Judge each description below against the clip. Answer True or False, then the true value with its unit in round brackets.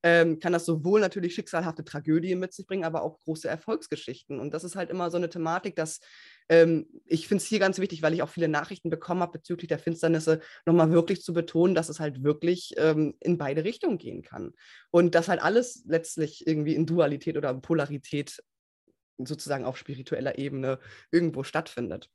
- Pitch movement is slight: True (2.3 semitones)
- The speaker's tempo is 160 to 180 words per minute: False (190 wpm)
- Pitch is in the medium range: True (165 Hz)